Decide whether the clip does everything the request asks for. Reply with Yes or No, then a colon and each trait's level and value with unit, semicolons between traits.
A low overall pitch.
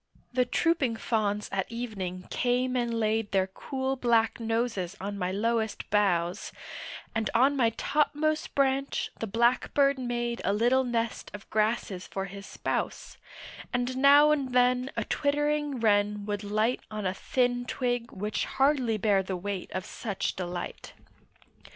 No: high, 230 Hz